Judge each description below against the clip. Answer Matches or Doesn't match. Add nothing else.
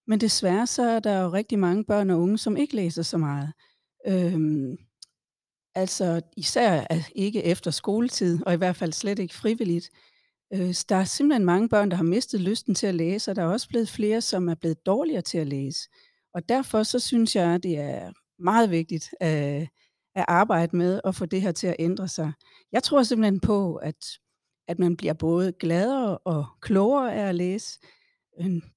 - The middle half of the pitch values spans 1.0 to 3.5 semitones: Doesn't match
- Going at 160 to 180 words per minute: Doesn't match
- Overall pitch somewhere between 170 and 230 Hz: Matches